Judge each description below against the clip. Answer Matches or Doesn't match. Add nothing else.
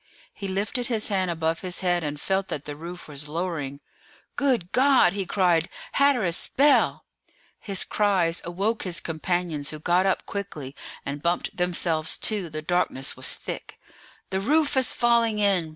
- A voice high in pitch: Doesn't match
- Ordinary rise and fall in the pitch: Matches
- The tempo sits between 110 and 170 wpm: Matches